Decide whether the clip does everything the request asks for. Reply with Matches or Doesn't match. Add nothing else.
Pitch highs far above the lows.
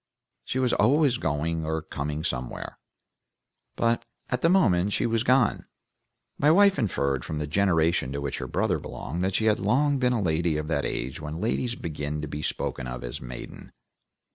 Matches